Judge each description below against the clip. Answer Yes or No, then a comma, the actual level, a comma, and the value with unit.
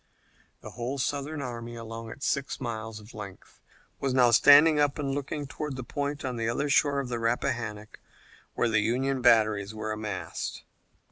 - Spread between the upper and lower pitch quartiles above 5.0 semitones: No, average, 3.9 semitones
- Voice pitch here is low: Yes, low, 120 Hz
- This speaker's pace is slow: No, average, 175 wpm